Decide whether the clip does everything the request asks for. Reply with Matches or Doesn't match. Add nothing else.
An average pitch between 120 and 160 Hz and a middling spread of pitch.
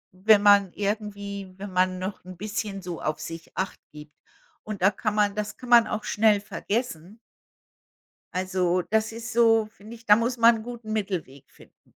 Doesn't match